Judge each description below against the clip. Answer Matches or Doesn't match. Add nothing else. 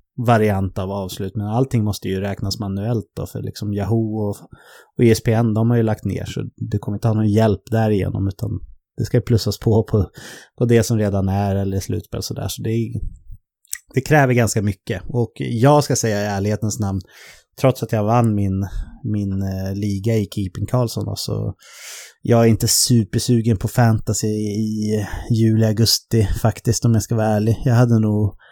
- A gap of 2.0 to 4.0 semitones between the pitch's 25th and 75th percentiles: Matches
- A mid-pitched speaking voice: Doesn't match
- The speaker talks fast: Doesn't match